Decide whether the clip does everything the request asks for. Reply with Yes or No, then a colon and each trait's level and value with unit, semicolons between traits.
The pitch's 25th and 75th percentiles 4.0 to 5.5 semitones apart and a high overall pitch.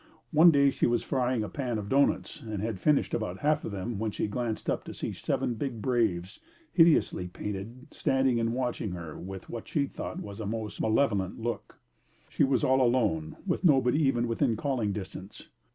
No: average, 4.3 semitones; low, 115 Hz